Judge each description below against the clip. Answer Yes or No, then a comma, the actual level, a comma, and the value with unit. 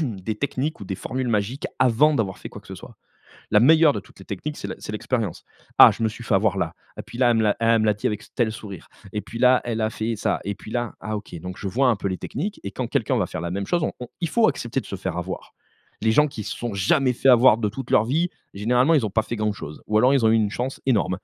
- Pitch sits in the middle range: No, low, 115 Hz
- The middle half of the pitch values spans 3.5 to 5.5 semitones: Yes, average, 3.9 semitones